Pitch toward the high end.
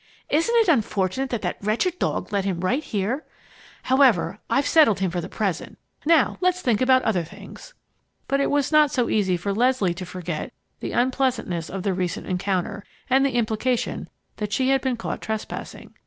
Yes: high, 225 Hz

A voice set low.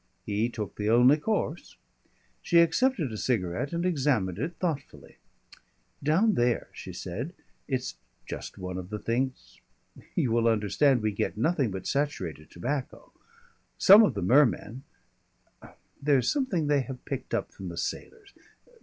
Yes: low, 130 Hz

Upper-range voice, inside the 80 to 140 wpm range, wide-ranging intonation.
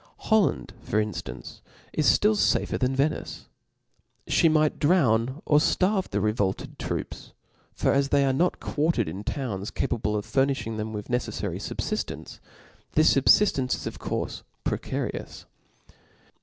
No: low, 135 Hz; slow, 135 wpm; wide, 6.2 semitones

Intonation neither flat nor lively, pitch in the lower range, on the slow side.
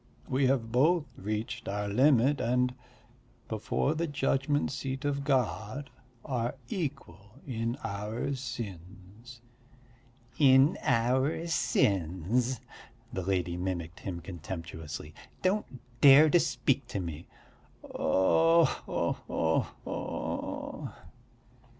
No: wide, 6.3 semitones; low, 120 Hz; slow, 100 wpm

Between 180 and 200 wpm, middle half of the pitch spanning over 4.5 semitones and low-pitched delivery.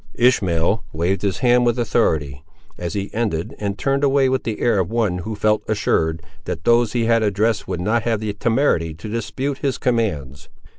Yes: average, 190 wpm; average, 5.0 semitones; low, 105 Hz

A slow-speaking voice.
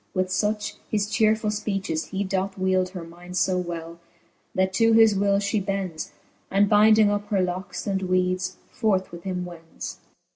No: average, 170 wpm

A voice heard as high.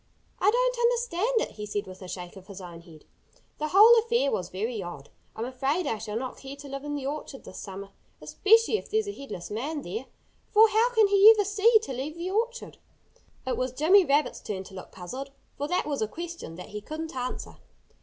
Yes: very high, 280 Hz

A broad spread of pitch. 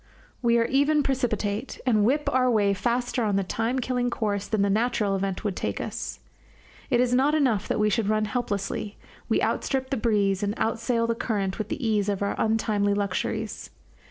No: average, 3.4 semitones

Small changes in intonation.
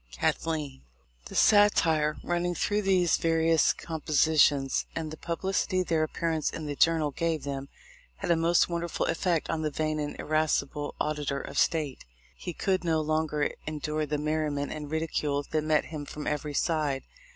Yes: narrow, 1.8 semitones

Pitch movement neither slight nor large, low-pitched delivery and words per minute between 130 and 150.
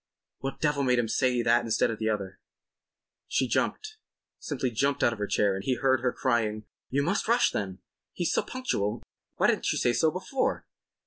No: average, 4.7 semitones; low, 125 Hz; average, 190 wpm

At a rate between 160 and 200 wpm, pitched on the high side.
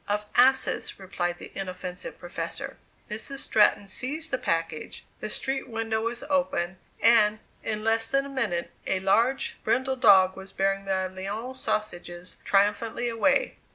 No: average, 145 wpm; high, 215 Hz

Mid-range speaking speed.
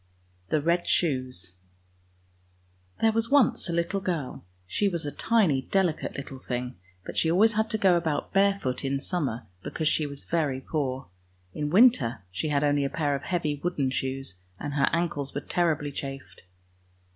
Yes: average, 170 wpm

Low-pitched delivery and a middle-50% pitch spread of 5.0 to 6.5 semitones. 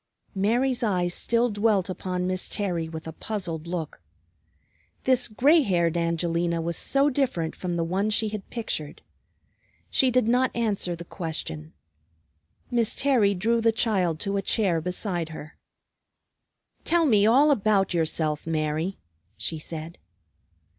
No: high, 190 Hz; wide, 5.4 semitones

